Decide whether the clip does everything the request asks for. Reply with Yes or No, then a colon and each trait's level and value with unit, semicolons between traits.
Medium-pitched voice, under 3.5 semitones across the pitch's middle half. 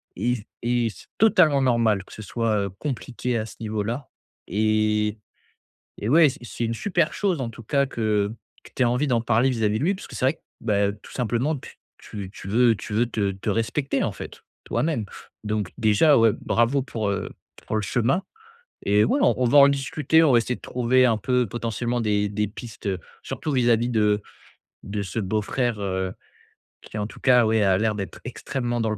No: low, 115 Hz; average, 3.1 semitones